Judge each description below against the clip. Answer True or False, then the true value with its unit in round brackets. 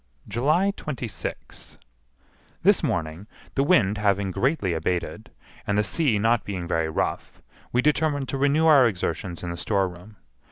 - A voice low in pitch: True (105 Hz)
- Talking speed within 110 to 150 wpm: True (145 wpm)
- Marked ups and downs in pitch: True (7.6 semitones)